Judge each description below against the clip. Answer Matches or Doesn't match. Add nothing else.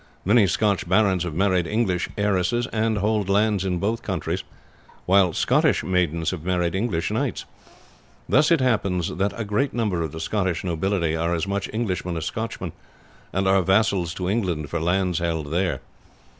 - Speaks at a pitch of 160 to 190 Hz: Doesn't match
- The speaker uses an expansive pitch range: Doesn't match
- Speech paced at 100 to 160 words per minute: Doesn't match